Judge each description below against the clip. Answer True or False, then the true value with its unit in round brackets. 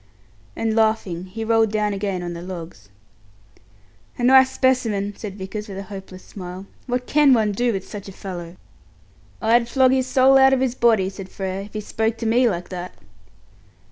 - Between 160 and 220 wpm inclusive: True (185 wpm)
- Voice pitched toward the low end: False (210 Hz)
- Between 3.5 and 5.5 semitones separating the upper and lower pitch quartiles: True (4.2 semitones)